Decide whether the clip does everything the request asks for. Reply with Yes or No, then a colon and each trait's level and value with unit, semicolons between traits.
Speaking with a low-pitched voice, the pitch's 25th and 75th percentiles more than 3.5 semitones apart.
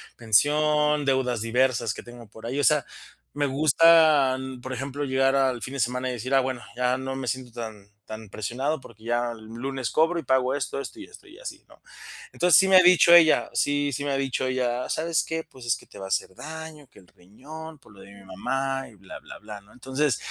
Yes: low, 130 Hz; average, 4.0 semitones